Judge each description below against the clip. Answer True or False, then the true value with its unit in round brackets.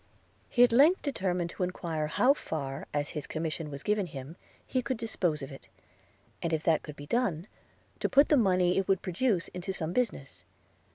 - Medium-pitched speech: True (180 Hz)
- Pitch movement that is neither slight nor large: False (6.9 semitones)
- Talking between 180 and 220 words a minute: True (190 wpm)